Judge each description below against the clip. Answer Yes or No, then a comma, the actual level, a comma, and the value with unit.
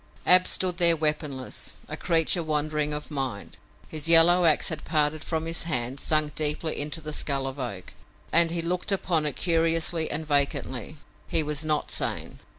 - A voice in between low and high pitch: Yes, medium, 155 Hz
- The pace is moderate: Yes, average, 170 wpm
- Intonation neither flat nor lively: No, narrow, 2.0 semitones